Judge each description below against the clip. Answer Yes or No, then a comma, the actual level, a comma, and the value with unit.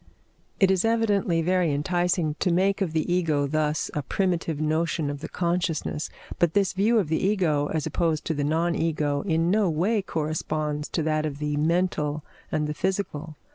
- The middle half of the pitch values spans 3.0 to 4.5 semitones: Yes, average, 3.3 semitones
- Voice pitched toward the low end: No, medium, 165 Hz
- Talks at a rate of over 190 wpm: No, average, 180 wpm